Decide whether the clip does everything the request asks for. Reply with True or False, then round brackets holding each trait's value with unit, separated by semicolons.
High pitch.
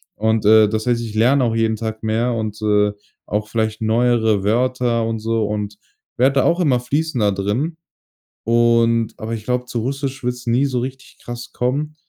False (115 Hz)